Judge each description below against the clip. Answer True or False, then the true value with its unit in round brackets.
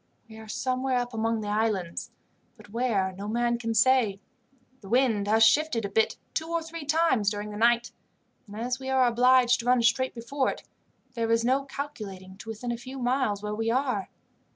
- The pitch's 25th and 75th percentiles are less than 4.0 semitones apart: True (3.2 semitones)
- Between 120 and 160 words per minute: False (200 wpm)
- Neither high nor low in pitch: False (235 Hz)